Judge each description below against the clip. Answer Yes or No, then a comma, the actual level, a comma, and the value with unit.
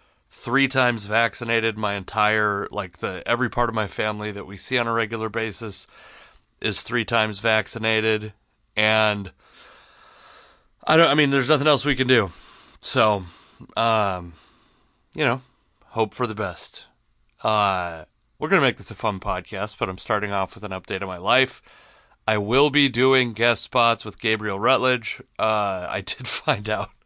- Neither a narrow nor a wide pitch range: No, narrow, 2.3 semitones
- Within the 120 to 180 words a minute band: Yes, average, 165 wpm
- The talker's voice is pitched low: Yes, low, 110 Hz